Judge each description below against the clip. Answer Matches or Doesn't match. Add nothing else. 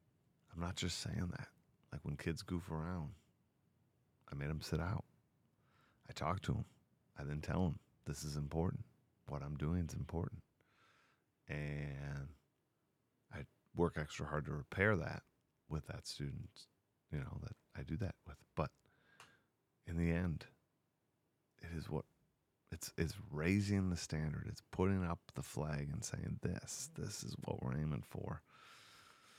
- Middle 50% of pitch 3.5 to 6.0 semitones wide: Matches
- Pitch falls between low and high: Doesn't match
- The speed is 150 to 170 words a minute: Matches